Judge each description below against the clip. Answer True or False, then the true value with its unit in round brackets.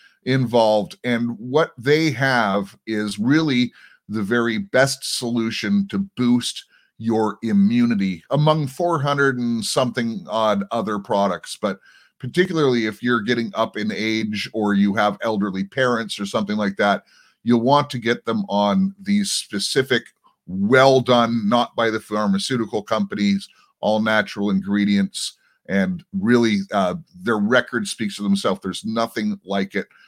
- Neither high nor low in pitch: False (115 Hz)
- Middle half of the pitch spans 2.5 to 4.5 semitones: False (5.0 semitones)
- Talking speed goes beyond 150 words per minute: False (140 wpm)